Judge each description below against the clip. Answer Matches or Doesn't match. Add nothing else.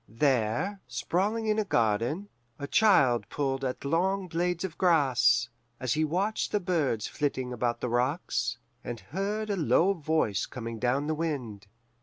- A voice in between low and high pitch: Matches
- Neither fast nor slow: Matches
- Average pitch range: Doesn't match